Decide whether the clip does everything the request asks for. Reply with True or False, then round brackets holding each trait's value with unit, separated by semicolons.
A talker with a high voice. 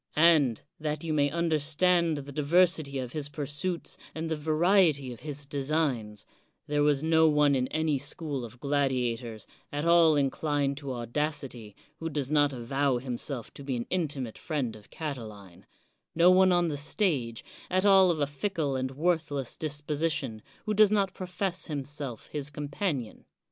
False (145 Hz)